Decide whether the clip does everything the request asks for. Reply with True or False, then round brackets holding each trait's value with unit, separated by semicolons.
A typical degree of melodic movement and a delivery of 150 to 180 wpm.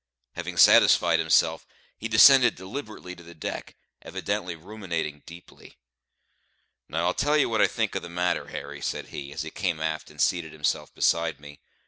True (4.1 semitones; 170 wpm)